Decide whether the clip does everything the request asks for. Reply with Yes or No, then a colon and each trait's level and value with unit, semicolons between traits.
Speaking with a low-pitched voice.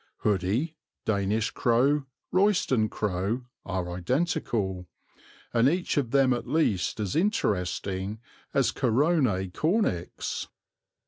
Yes: low, 115 Hz